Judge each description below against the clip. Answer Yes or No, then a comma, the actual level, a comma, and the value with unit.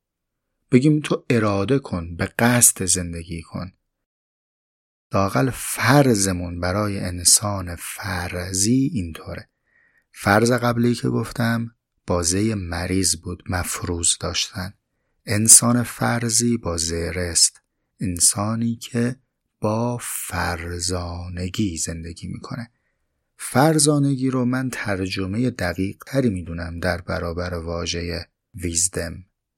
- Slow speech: Yes, slow, 90 wpm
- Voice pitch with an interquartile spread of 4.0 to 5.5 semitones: Yes, average, 5.2 semitones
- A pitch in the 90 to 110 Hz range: Yes, very low, 95 Hz